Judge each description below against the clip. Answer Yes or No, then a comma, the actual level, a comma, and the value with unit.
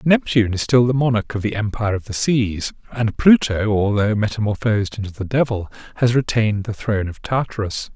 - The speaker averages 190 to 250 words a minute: No, average, 180 wpm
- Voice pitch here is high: No, low, 110 Hz